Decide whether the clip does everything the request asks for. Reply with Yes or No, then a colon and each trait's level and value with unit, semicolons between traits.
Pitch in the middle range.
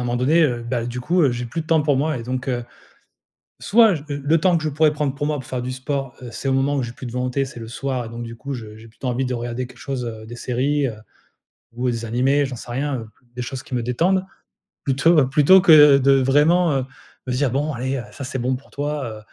No: low, 130 Hz